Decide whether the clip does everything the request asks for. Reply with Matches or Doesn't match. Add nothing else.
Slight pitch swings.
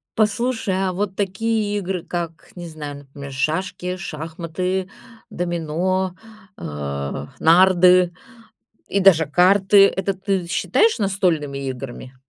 Doesn't match